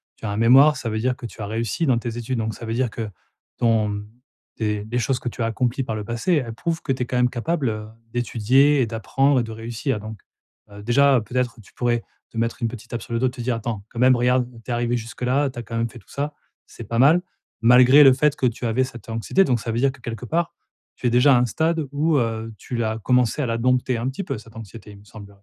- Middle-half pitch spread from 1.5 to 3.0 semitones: Yes, narrow, 2.5 semitones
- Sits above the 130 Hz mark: No, low, 120 Hz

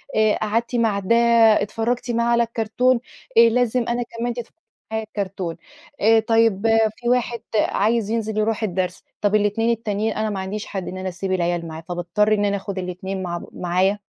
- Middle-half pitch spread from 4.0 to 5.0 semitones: No, average, 3.3 semitones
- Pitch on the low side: No, high, 215 Hz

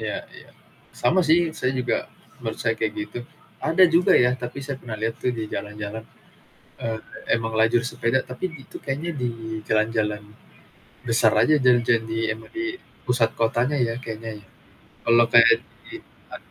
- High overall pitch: No, low, 115 Hz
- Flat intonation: Yes, narrow, 2.2 semitones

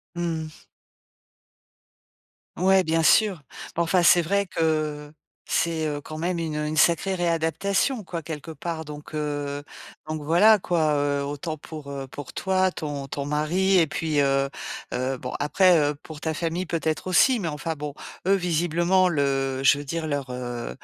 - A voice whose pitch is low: No, medium, 160 Hz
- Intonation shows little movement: No, average, 3.1 semitones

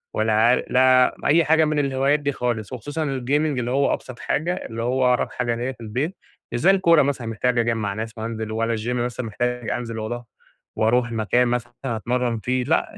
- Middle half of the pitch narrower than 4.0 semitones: Yes, average, 2.9 semitones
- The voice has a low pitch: Yes, low, 125 Hz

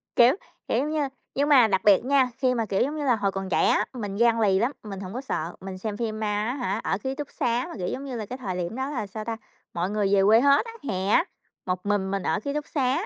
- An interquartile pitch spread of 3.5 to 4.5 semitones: No, average, 5.2 semitones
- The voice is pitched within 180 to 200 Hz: No, high, 225 Hz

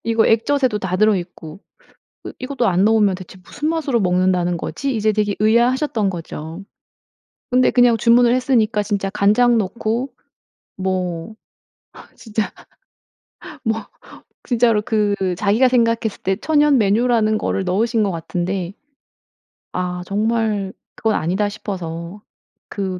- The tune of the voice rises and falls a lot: No, average, 3.8 semitones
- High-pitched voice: Yes, high, 215 Hz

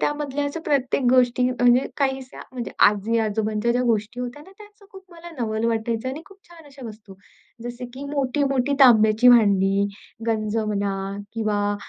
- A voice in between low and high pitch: No, high, 245 Hz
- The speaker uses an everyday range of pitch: Yes, average, 4.2 semitones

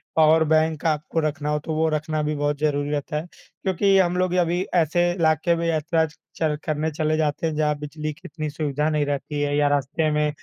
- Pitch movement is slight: Yes, narrow, 1.5 semitones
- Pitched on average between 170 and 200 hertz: No, medium, 155 Hz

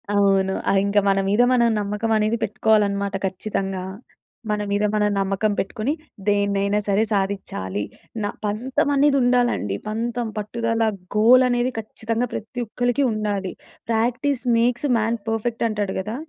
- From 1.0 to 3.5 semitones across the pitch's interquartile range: Yes, average, 2.8 semitones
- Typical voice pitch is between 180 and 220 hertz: Yes, high, 215 Hz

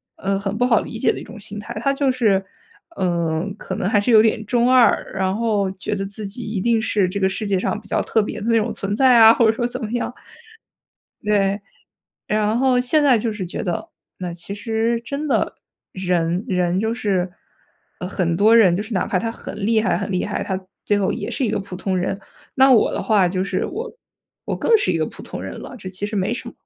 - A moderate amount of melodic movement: Yes, average, 3.3 semitones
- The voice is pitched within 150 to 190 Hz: No, high, 210 Hz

